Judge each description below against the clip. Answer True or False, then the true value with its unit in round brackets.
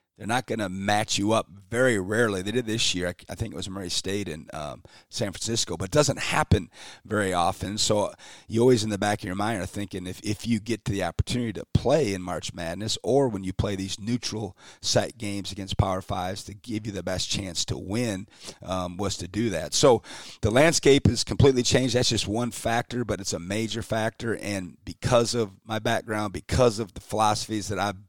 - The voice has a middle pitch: False (105 Hz)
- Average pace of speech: False (220 wpm)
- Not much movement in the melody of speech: False (3.2 semitones)